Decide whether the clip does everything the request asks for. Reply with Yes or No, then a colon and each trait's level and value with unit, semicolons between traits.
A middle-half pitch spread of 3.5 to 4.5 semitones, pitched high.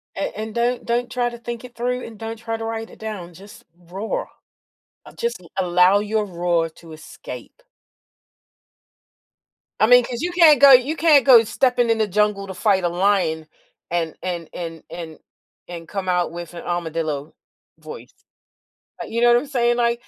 No: average, 5.3 semitones; high, 215 Hz